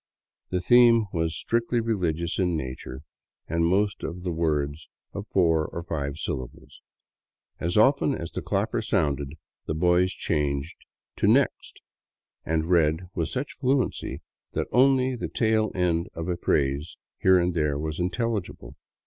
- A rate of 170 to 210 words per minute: No, average, 150 wpm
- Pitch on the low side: Yes, very low, 85 Hz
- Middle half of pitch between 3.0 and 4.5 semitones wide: No, average, 5.1 semitones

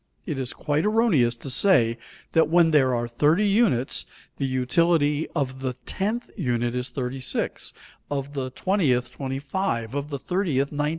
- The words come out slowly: No, average, 155 wpm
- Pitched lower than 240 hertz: Yes, medium, 140 Hz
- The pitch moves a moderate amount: Yes, average, 4.8 semitones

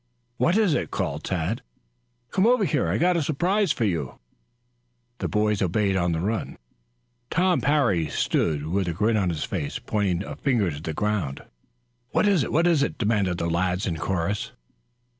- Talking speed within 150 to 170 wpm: No, average, 180 wpm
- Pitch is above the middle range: No, low, 100 Hz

